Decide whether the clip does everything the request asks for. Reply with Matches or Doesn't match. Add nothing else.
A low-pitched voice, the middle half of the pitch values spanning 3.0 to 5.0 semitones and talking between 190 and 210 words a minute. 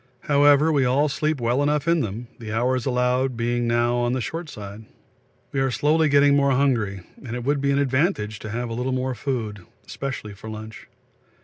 Matches